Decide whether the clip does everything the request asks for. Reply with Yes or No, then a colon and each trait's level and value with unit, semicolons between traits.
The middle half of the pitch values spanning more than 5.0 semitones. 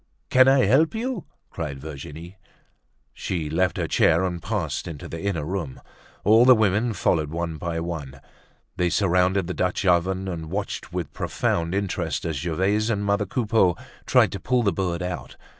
No: average, 3.6 semitones